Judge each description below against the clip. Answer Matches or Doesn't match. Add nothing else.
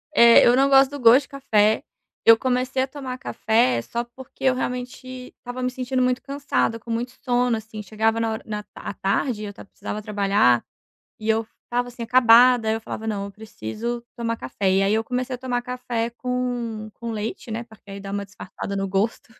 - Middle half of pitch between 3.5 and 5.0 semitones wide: Doesn't match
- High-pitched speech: Matches